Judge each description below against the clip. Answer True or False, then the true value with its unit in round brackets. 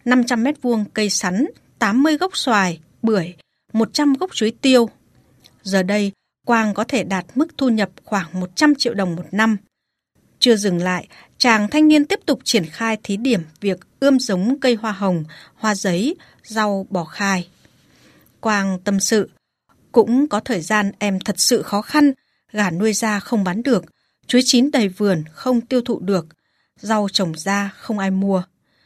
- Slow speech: False (175 wpm)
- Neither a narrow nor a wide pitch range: True (4.4 semitones)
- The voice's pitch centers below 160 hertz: False (215 Hz)